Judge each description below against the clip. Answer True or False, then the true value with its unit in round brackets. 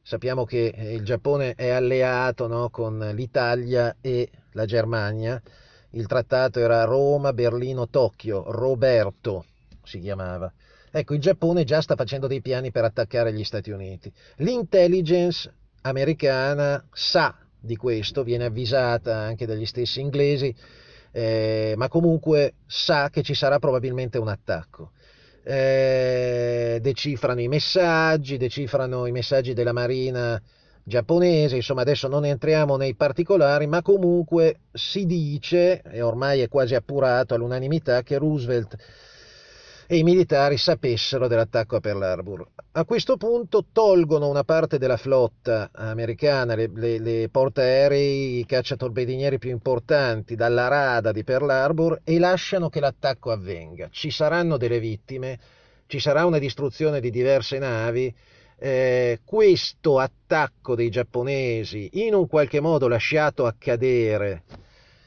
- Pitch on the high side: False (130 Hz)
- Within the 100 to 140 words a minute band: True (130 wpm)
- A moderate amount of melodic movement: True (3.6 semitones)